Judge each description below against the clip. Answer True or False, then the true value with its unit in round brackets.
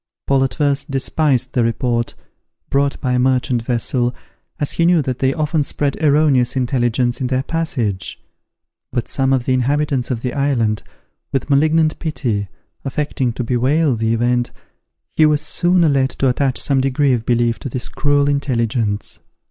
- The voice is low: True (130 Hz)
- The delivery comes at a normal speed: True (165 wpm)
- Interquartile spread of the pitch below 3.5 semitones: True (2.9 semitones)